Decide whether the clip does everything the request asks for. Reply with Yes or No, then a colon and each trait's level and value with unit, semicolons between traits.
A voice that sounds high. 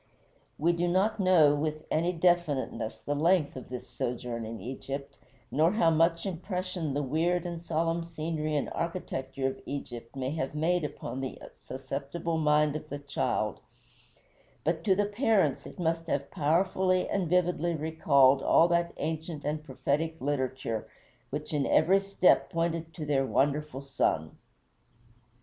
No: medium, 155 Hz